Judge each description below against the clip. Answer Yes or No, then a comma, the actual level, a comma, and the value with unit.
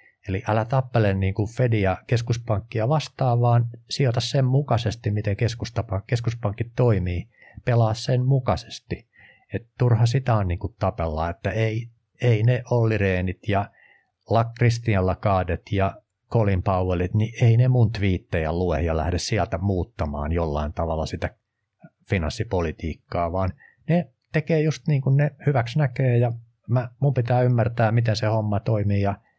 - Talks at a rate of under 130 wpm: No, average, 135 wpm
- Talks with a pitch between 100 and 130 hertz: Yes, low, 110 Hz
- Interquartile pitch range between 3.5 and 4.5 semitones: Yes, average, 4.2 semitones